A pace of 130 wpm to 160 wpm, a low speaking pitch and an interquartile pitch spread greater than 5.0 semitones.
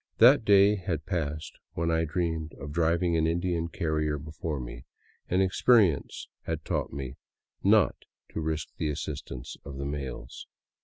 No: average, 150 wpm; very low, 80 Hz; average, 3.0 semitones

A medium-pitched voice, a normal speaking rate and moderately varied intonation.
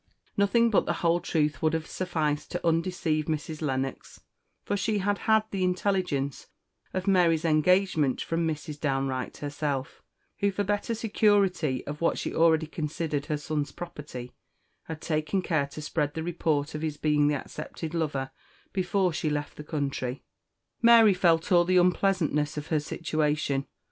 Yes: medium, 160 Hz; average, 160 wpm; average, 3.5 semitones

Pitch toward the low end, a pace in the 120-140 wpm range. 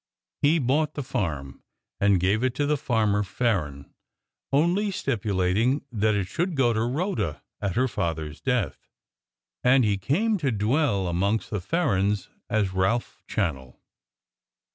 Yes: low, 110 Hz; slow, 135 wpm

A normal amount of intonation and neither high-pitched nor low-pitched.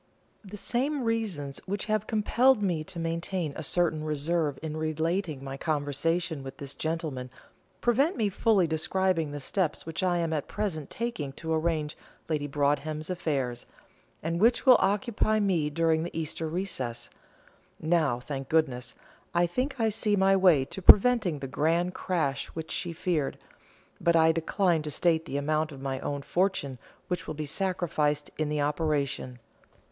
Yes: average, 4.2 semitones; medium, 160 Hz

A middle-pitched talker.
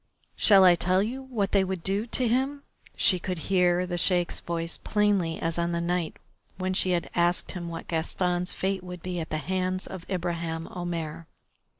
Yes: medium, 180 Hz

